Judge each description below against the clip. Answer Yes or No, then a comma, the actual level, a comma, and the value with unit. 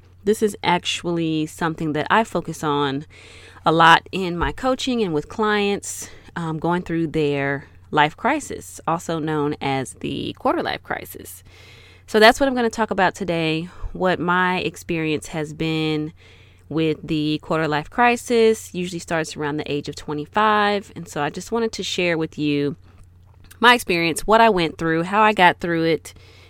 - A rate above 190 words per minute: No, average, 170 wpm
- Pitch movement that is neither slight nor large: Yes, average, 4.0 semitones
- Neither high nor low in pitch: Yes, medium, 160 Hz